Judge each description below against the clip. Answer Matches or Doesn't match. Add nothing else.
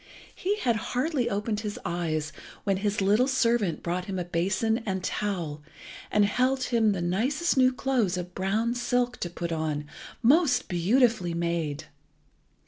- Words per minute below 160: Matches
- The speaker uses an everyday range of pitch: Doesn't match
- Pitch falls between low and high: Doesn't match